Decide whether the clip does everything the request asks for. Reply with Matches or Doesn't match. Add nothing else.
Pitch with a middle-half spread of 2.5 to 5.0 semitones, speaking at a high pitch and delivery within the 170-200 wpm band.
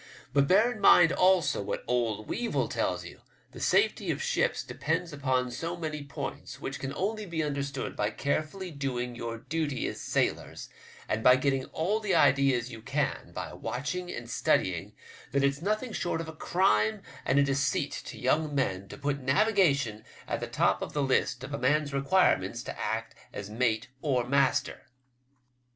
Doesn't match